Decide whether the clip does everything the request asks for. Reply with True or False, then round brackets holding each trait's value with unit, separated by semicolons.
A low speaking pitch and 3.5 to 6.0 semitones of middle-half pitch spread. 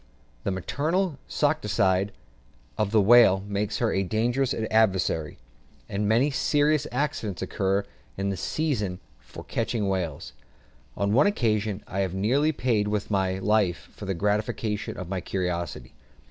True (105 Hz; 3.8 semitones)